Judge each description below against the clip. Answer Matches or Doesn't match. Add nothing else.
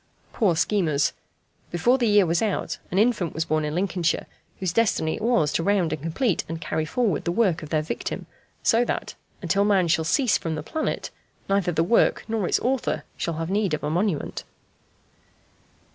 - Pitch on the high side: Doesn't match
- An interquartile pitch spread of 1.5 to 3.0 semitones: Doesn't match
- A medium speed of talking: Matches